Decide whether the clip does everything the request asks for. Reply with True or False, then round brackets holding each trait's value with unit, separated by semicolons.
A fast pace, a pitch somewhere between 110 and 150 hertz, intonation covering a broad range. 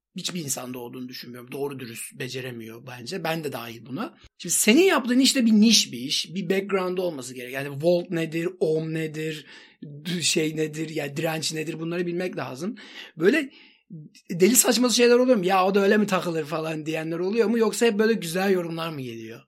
False (190 wpm; 170 Hz; 5.8 semitones)